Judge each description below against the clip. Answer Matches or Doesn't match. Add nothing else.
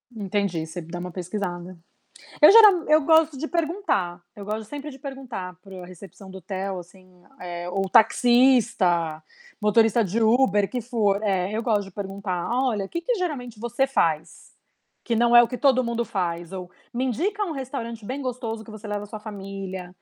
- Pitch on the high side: Matches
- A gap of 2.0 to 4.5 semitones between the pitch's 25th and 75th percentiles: Doesn't match